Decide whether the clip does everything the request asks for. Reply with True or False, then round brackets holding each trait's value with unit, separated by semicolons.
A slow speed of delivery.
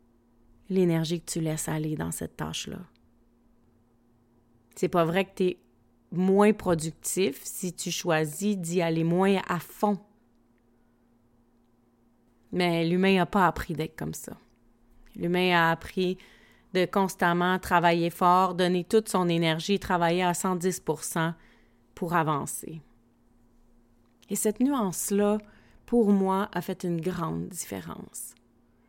True (120 wpm)